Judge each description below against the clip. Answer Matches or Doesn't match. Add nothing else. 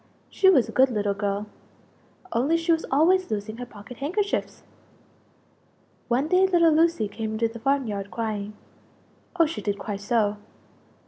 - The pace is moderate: Matches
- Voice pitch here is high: Matches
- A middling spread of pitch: Doesn't match